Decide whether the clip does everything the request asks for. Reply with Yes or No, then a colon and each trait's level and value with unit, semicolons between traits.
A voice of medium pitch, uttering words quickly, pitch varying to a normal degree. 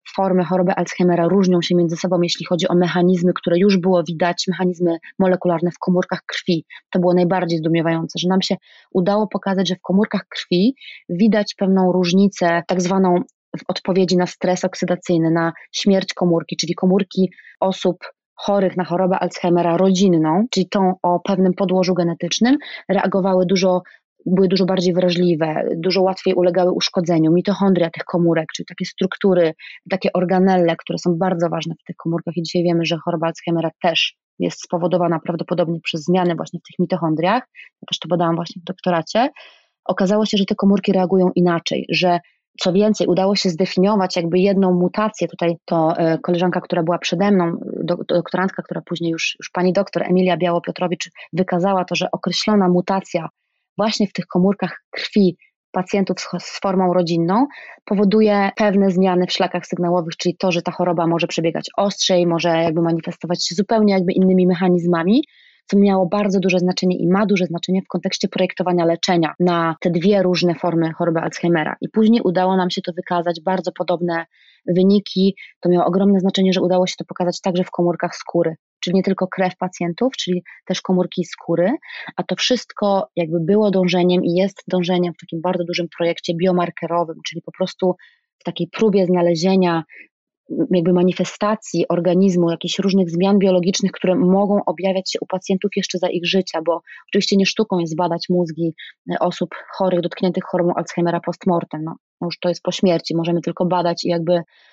No: medium, 180 Hz; fast, 165 wpm; narrow, 1.7 semitones